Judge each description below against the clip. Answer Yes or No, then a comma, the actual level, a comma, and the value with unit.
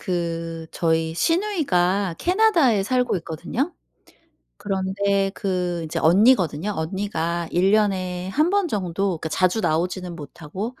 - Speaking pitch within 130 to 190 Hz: Yes, medium, 185 Hz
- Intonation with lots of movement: No, average, 4.0 semitones